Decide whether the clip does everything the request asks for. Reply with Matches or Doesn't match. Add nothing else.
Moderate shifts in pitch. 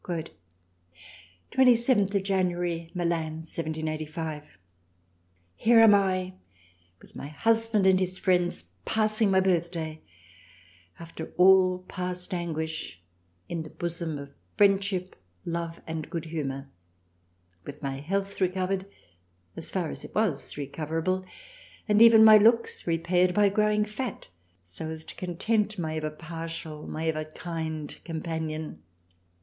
Matches